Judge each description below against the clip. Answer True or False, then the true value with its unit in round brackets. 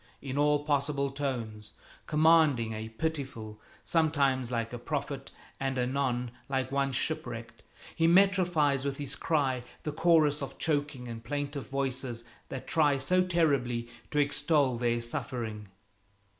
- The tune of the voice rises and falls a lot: False (3.3 semitones)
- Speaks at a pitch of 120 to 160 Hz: True (140 Hz)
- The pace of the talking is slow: True (130 wpm)